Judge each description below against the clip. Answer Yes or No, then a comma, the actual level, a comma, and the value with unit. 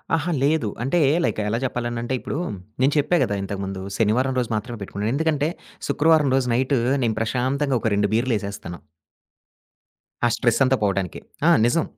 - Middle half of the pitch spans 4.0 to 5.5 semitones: Yes, average, 4.6 semitones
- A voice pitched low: Yes, low, 125 Hz